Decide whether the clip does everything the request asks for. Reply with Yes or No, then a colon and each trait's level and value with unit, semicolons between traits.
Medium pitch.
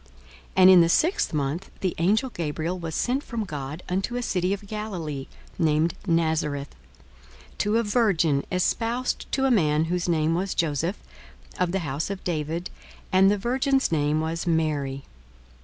Yes: medium, 175 Hz